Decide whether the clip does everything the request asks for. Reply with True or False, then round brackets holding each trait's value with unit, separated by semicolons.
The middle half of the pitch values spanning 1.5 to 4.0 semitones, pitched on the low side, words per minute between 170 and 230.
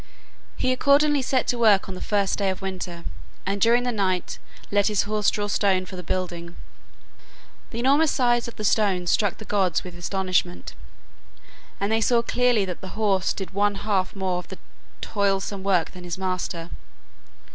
False (3.1 semitones; 200 Hz; 180 wpm)